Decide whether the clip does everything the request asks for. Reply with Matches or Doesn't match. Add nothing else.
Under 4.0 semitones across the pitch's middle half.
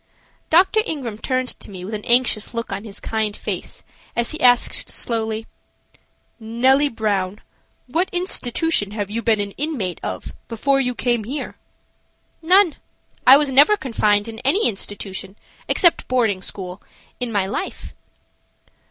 Doesn't match